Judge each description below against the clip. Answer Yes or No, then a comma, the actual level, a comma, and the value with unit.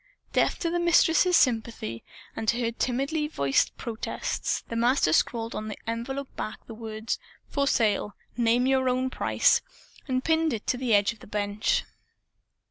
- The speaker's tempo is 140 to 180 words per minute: Yes, average, 165 wpm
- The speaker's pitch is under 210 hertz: No, high, 235 Hz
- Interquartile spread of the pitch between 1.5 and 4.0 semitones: Yes, average, 3.7 semitones